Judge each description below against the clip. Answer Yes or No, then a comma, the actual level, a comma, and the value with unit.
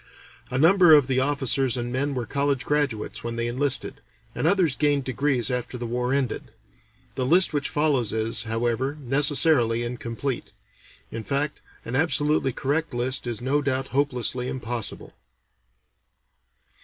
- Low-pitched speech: Yes, low, 130 Hz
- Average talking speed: Yes, average, 145 wpm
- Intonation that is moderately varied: Yes, average, 3.2 semitones